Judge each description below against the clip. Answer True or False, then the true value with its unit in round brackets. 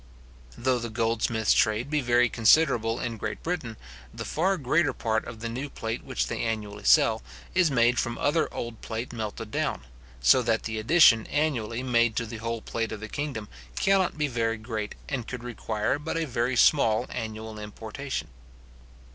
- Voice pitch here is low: True (115 Hz)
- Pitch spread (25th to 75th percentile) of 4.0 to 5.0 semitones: False (3.0 semitones)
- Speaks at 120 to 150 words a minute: False (175 wpm)